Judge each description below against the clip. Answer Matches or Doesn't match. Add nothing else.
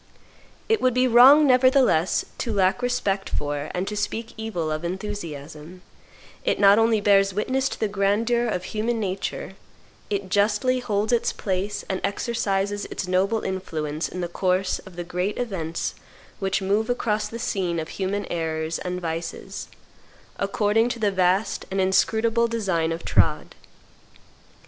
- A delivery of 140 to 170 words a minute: Matches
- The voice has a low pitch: Doesn't match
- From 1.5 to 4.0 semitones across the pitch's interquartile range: Matches